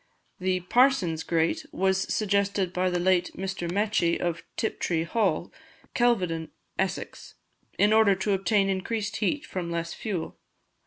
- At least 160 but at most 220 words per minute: No, slow, 135 wpm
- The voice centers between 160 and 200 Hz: Yes, high, 190 Hz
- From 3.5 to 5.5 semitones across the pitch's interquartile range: No, average, 2.9 semitones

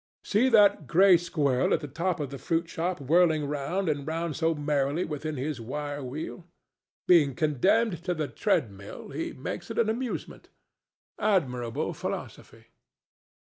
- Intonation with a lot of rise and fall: No, average, 3.8 semitones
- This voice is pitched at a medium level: Yes, medium, 155 Hz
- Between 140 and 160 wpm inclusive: Yes, average, 145 wpm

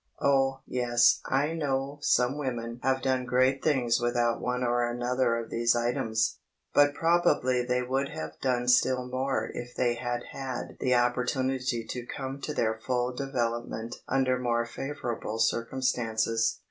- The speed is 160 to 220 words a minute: No, average, 145 wpm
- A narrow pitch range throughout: Yes, narrow, 2.0 semitones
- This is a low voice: Yes, low, 125 Hz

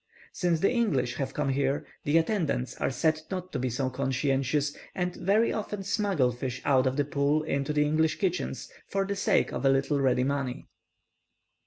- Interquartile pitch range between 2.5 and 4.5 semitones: No, average, 5.0 semitones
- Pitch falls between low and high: Yes, medium, 145 Hz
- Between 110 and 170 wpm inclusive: No, average, 185 wpm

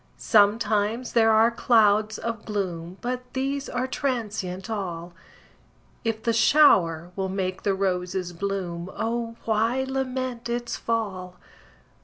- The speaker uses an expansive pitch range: No, average, 4.0 semitones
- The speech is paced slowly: Yes, slow, 120 wpm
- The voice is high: Yes, high, 215 Hz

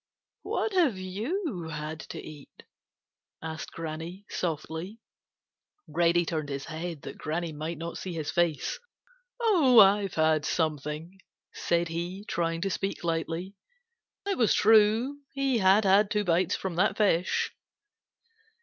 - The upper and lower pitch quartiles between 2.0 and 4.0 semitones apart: No, average, 4.4 semitones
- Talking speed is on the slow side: Yes, slow, 130 wpm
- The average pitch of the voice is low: No, medium, 175 Hz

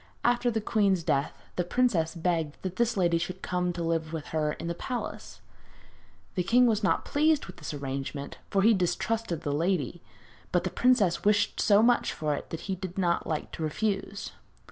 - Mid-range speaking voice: Yes, medium, 180 Hz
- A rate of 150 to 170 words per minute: No, average, 195 wpm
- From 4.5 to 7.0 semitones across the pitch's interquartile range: Yes, average, 4.8 semitones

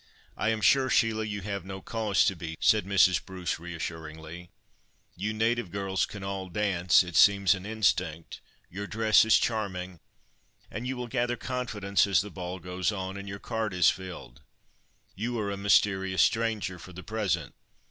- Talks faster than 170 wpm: No, average, 165 wpm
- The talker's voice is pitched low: Yes, low, 100 Hz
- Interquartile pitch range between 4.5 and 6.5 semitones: No, average, 3.1 semitones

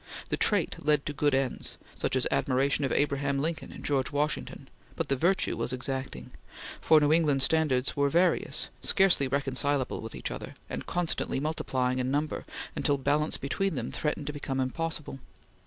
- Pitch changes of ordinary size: No, narrow, 2.3 semitones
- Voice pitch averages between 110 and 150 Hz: Yes, medium, 140 Hz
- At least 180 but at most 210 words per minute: No, average, 170 wpm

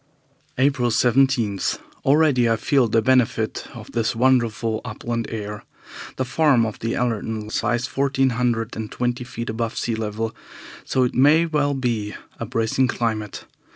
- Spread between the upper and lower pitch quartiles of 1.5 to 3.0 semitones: Yes, average, 2.7 semitones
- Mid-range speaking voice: No, low, 120 Hz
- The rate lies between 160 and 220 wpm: No, average, 150 wpm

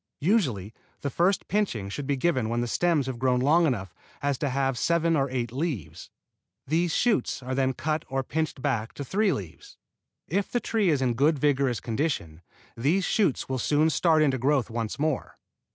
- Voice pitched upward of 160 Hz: No, medium, 140 Hz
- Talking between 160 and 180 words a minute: No, average, 190 wpm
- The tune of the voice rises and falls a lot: No, average, 4.5 semitones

